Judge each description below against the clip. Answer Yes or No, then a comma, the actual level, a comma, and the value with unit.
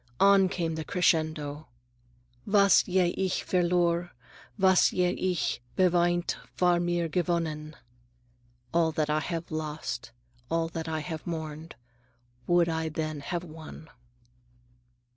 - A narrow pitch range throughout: Yes, narrow, 2.1 semitones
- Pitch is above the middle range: No, medium, 170 Hz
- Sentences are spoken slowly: Yes, slow, 120 wpm